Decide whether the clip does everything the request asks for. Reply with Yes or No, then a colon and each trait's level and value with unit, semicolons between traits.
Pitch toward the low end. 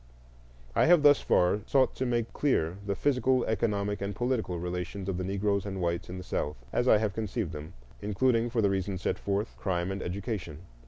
Yes: low, 100 Hz